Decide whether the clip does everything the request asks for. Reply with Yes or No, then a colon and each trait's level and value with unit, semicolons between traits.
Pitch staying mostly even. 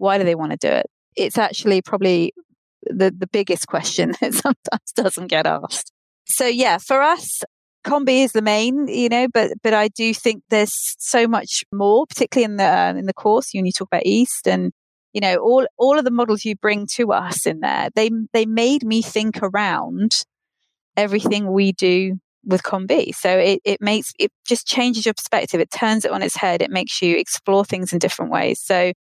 No: average, 3.8 semitones